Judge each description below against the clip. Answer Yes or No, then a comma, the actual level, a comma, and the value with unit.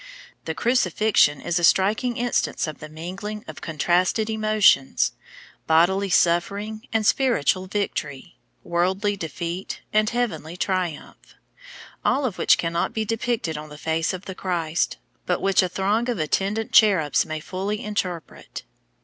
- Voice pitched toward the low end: No, medium, 185 Hz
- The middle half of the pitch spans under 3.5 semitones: No, average, 4.3 semitones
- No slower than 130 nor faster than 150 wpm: Yes, average, 140 wpm